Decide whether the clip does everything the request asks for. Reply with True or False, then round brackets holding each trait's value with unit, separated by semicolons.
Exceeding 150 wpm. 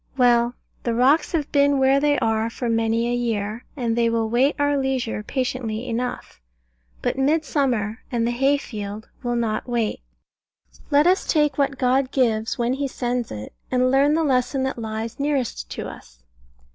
True (170 wpm)